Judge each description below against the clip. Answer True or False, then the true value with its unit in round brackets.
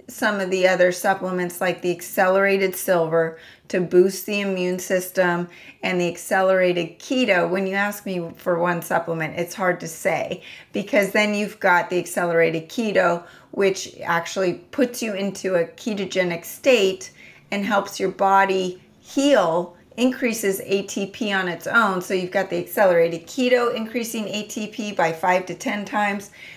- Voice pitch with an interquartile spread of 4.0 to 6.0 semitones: False (2.7 semitones)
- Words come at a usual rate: True (150 wpm)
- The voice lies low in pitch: False (190 Hz)